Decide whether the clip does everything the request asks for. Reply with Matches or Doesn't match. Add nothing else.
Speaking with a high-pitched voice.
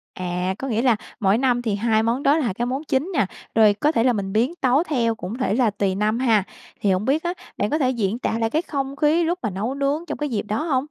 Matches